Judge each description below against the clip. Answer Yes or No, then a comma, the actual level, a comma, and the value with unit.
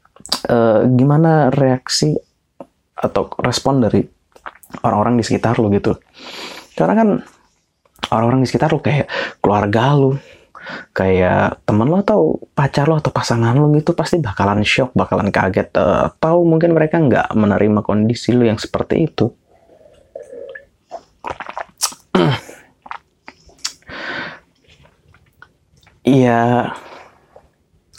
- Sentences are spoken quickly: No, average, 105 wpm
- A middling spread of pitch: No, wide, 5.8 semitones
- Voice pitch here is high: No, low, 120 Hz